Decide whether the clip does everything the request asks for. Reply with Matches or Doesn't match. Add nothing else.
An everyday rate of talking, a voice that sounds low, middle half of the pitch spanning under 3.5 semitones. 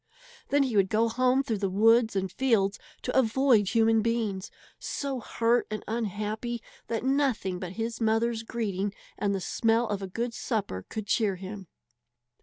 Doesn't match